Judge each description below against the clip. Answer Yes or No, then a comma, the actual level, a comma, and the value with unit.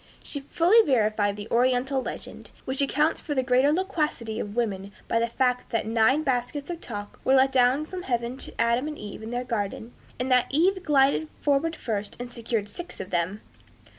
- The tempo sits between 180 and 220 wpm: Yes, average, 195 wpm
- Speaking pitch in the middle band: No, very high, 250 Hz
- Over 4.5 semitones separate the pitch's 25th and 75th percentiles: No, average, 4.1 semitones